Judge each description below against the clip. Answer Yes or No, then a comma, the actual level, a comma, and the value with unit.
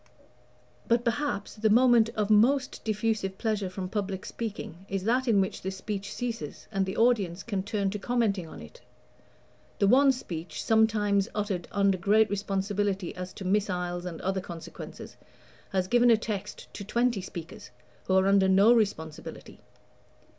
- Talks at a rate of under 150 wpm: No, average, 155 wpm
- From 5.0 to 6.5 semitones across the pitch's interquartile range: No, average, 2.8 semitones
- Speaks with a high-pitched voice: Yes, high, 200 Hz